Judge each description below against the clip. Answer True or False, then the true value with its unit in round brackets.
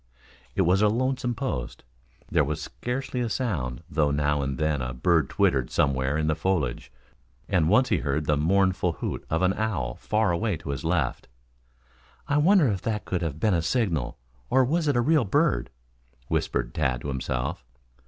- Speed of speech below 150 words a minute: False (185 wpm)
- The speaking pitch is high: False (85 Hz)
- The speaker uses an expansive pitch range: True (7.8 semitones)